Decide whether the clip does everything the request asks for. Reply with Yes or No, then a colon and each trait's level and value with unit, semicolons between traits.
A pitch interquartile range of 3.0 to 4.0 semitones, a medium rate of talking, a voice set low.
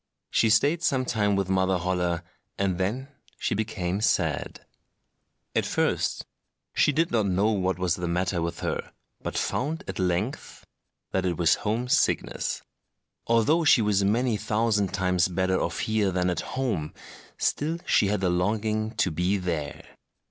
Yes: average, 3.6 semitones; average, 155 wpm; low, 100 Hz